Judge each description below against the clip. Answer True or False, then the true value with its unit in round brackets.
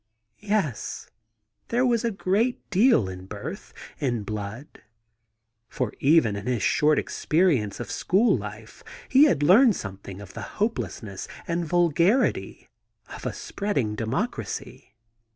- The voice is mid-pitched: True (150 Hz)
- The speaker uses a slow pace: True (125 wpm)